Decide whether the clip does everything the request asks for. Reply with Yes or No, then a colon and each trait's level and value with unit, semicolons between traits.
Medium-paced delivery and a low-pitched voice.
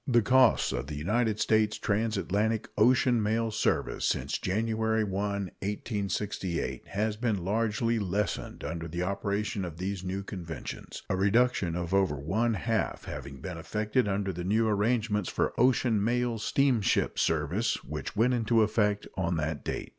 Yes: average, 150 wpm; low, 105 Hz